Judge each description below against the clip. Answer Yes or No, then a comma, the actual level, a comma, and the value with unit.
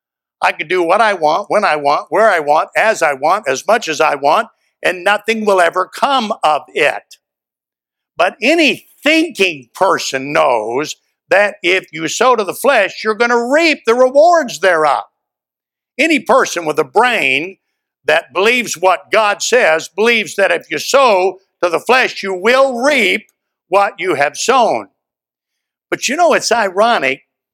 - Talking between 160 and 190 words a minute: Yes, average, 165 wpm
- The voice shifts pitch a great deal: Yes, wide, 7.1 semitones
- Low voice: No, high, 210 Hz